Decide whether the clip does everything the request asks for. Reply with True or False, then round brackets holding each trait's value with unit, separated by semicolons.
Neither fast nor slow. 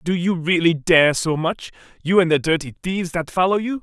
False (220 wpm)